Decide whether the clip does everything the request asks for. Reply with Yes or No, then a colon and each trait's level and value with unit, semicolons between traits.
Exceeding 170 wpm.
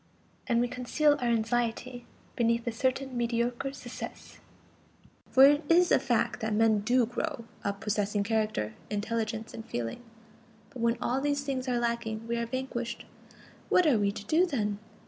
No: average, 165 wpm